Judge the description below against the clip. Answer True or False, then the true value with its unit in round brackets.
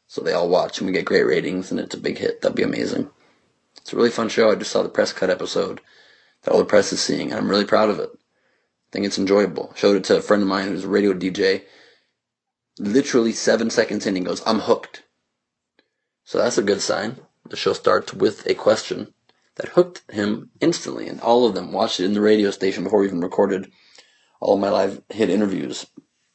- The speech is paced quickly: True (225 wpm)